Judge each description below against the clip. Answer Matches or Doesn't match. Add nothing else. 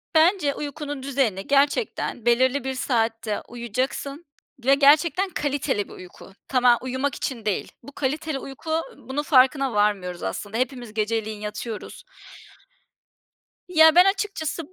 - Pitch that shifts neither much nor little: Matches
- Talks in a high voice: Matches